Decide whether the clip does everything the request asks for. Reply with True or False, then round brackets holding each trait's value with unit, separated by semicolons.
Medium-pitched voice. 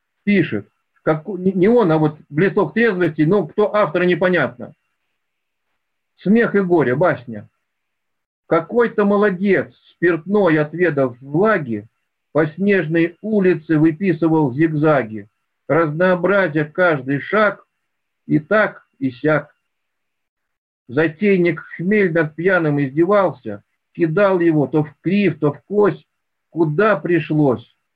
True (170 Hz)